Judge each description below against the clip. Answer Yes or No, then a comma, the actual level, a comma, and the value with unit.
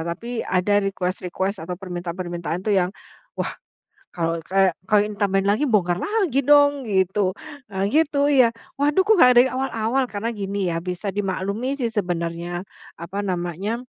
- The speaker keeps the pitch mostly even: No, average, 5.2 semitones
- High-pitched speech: Yes, high, 200 Hz